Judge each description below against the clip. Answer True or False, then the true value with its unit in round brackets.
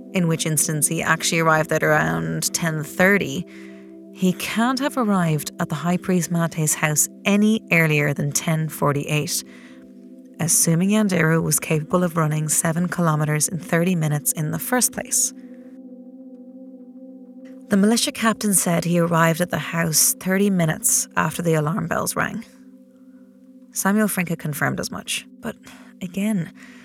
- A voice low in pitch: False (175 Hz)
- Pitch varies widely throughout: True (7.2 semitones)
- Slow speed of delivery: False (145 wpm)